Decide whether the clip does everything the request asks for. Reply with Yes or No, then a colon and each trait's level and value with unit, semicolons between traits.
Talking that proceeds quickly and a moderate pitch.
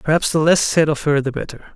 Yes: fast, 275 wpm; medium, 150 Hz